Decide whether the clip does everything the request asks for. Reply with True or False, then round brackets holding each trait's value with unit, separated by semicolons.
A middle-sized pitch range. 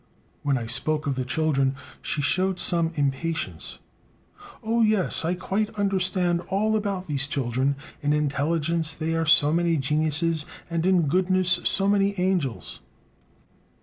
True (4.2 semitones)